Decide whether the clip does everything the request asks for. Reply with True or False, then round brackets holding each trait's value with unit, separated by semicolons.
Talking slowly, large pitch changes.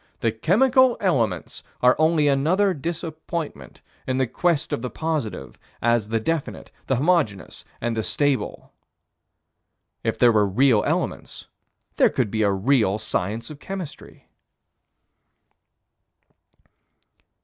True (115 wpm; 6.7 semitones)